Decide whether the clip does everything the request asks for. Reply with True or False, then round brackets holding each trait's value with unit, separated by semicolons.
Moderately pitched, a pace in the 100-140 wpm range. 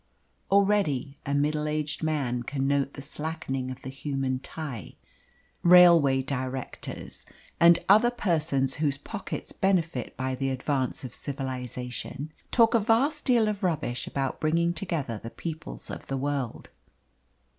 True (145 Hz; 135 wpm)